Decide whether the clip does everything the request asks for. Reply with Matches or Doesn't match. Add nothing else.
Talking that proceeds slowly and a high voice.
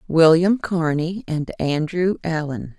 Doesn't match